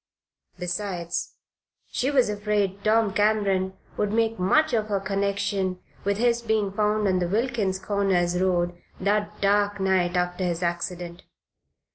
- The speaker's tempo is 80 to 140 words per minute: Yes, slow, 135 wpm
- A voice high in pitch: Yes, high, 200 Hz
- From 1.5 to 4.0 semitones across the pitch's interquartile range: Yes, narrow, 2.5 semitones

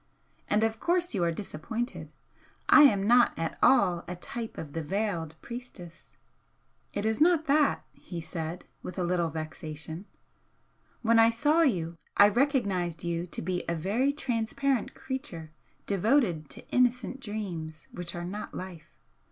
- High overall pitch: Yes, high, 200 Hz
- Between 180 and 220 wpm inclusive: No, average, 150 wpm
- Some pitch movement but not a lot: No, wide, 6.2 semitones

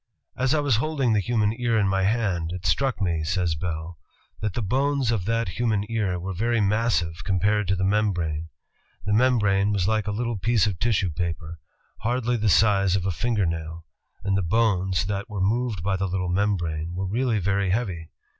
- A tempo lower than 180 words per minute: No, average, 195 wpm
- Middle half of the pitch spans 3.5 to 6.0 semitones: Yes, average, 4.0 semitones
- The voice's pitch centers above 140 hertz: No, low, 100 Hz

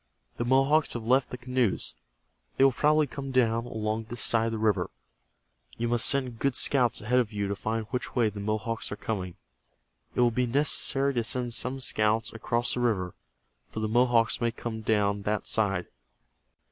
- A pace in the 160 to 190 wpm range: Yes, average, 185 wpm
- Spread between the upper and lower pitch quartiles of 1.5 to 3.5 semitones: Yes, narrow, 2.6 semitones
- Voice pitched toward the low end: Yes, low, 115 Hz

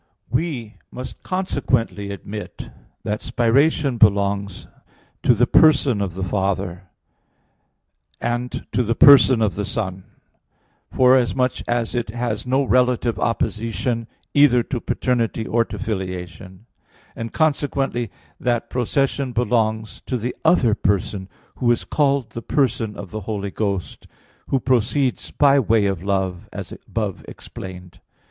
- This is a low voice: Yes, low, 115 Hz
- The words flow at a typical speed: No, slow, 125 wpm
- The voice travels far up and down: No, average, 4.0 semitones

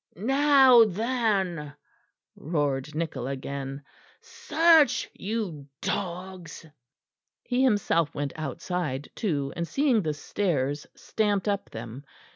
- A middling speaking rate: No, slow, 95 wpm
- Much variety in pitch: Yes, wide, 7.3 semitones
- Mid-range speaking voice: Yes, medium, 175 Hz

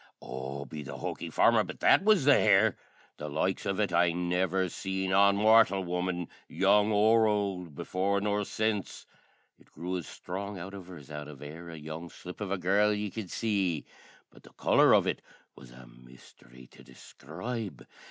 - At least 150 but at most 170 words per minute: No, average, 185 wpm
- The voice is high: No, very low, 95 Hz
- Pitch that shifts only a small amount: No, average, 4.4 semitones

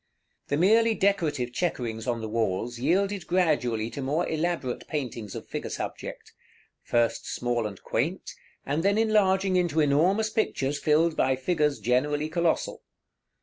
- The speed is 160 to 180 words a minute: No, average, 140 wpm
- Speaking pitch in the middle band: Yes, medium, 150 Hz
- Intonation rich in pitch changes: Yes, wide, 6.7 semitones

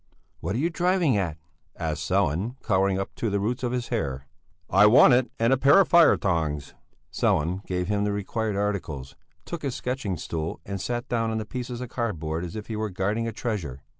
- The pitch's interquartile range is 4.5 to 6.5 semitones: Yes, average, 5.1 semitones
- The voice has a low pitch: Yes, low, 105 Hz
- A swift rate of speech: Yes, fast, 210 wpm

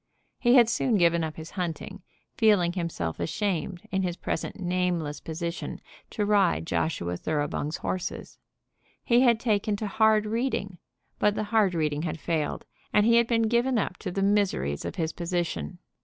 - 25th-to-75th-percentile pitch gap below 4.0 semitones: No, average, 4.7 semitones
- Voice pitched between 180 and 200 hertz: Yes, medium, 185 Hz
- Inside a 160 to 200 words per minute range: Yes, average, 165 wpm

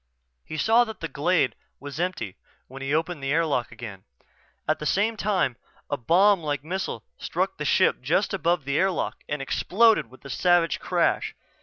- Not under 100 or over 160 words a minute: No, average, 175 wpm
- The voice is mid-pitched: Yes, medium, 160 Hz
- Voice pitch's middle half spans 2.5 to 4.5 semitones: No, average, 5.3 semitones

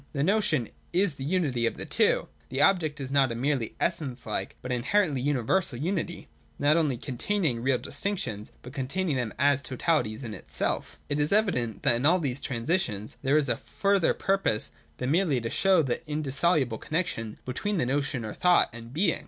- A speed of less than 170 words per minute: No, average, 185 wpm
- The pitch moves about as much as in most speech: No, wide, 5.7 semitones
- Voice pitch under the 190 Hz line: Yes, medium, 140 Hz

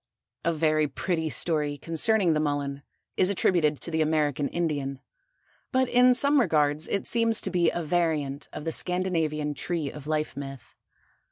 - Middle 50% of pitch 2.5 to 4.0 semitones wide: Yes, average, 3.2 semitones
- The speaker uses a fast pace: No, average, 160 wpm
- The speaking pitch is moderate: Yes, medium, 155 Hz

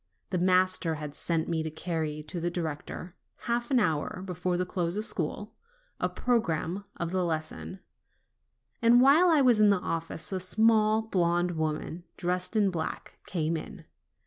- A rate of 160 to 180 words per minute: Yes, average, 165 wpm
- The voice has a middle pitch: Yes, medium, 180 Hz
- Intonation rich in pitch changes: No, average, 4.4 semitones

